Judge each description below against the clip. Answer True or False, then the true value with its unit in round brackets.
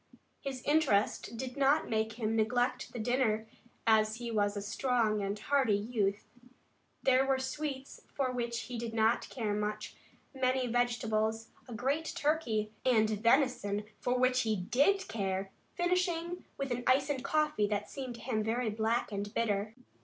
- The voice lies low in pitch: False (235 Hz)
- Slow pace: False (160 wpm)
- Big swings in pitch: False (3.5 semitones)